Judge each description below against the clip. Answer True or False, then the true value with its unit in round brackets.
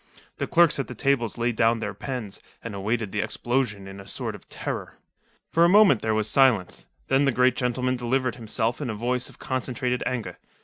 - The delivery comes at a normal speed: False (210 wpm)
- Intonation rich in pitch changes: False (3.0 semitones)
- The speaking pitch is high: False (120 Hz)